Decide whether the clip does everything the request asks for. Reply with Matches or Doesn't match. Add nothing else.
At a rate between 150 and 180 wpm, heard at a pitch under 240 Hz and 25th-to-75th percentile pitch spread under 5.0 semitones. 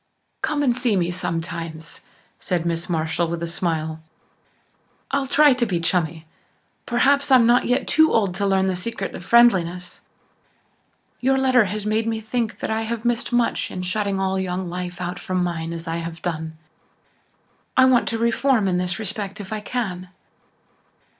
Doesn't match